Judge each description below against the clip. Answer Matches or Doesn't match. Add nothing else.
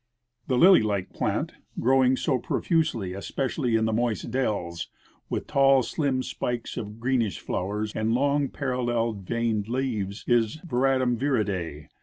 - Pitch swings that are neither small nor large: Matches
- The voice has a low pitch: Matches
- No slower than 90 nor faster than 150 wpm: Matches